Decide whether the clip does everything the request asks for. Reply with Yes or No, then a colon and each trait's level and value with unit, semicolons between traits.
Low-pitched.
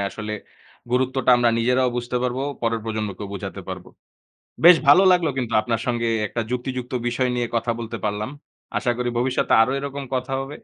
Yes: low, 125 Hz